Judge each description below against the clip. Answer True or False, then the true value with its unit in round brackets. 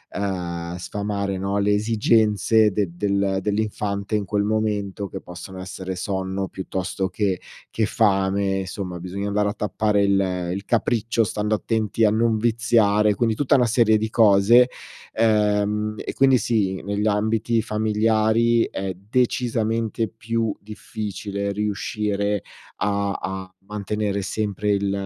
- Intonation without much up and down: True (2.0 semitones)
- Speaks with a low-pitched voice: True (105 Hz)